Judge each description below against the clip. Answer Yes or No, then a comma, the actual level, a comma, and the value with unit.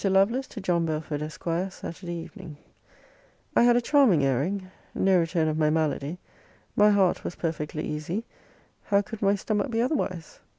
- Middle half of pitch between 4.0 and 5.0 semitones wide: Yes, average, 4.6 semitones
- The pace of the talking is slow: No, average, 160 wpm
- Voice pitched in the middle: Yes, medium, 180 Hz